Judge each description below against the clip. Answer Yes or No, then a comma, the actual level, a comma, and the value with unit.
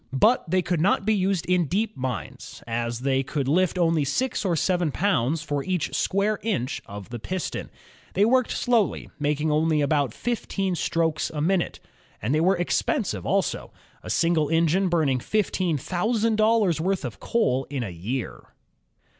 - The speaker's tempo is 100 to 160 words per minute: No, average, 170 wpm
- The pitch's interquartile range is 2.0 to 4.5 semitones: No, wide, 5.5 semitones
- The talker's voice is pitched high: No, medium, 165 Hz